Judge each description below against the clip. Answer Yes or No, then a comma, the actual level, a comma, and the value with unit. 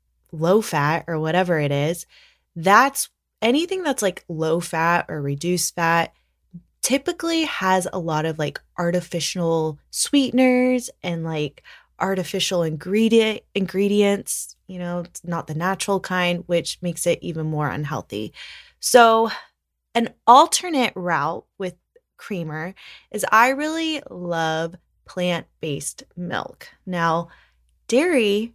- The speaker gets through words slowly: Yes, slow, 120 wpm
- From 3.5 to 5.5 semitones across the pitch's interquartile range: Yes, average, 4.8 semitones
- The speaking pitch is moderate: Yes, medium, 175 Hz